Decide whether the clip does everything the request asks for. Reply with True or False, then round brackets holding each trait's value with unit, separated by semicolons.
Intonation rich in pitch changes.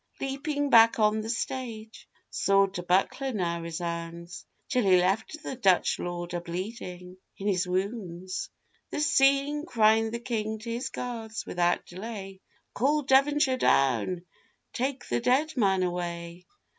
True (5.9 semitones)